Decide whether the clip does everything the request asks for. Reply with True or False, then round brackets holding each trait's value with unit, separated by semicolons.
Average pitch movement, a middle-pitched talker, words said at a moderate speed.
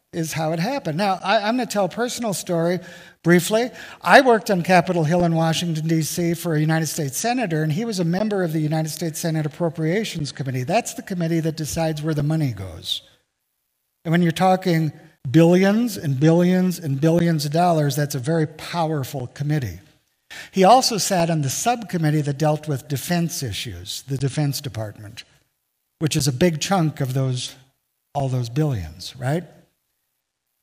True (3.6 semitones; 160 Hz; 175 wpm)